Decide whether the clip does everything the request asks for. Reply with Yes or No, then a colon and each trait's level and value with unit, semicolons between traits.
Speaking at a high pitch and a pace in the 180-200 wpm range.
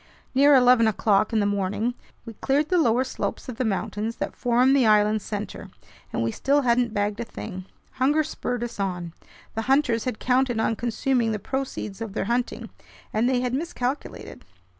Yes: high, 235 Hz; average, 185 wpm